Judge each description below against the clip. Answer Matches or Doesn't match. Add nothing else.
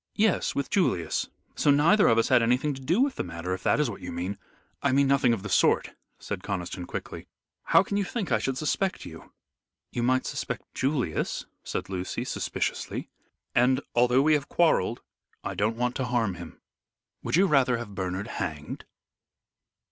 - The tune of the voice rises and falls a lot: Matches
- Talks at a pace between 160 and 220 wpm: Matches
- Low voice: Matches